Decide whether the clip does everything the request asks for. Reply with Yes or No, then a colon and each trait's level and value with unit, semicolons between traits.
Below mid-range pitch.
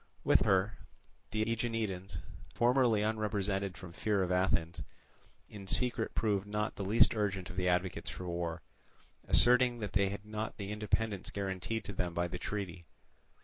Yes: low, 100 Hz